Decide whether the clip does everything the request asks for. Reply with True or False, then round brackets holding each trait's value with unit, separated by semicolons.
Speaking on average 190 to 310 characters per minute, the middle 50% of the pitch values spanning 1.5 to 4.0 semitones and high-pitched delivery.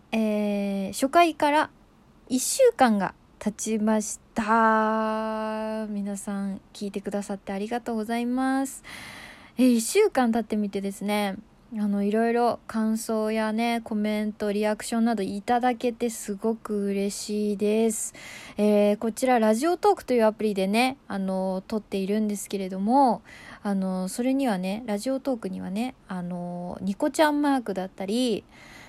True (295 characters per minute; 3.0 semitones; 220 Hz)